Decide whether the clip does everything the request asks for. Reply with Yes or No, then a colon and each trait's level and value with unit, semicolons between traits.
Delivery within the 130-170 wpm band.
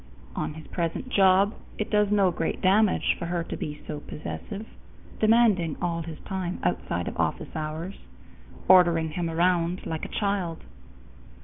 Yes: average, 150 wpm